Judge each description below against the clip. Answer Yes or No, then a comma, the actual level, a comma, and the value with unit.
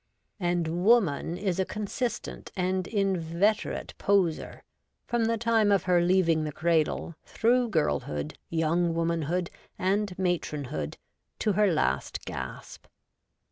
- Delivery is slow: Yes, slow, 120 wpm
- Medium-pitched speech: Yes, medium, 180 Hz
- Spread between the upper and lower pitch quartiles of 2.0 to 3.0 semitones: No, average, 3.7 semitones